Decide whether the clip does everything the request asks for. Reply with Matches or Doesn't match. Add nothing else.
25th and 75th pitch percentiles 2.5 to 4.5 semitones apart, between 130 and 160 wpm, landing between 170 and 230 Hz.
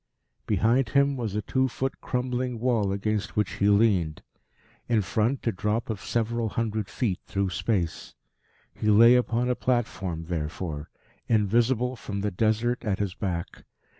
Doesn't match